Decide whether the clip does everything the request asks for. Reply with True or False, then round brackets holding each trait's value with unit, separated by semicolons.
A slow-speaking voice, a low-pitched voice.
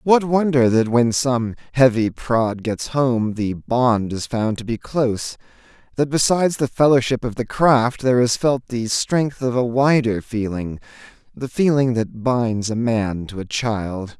False (170 wpm; 120 Hz)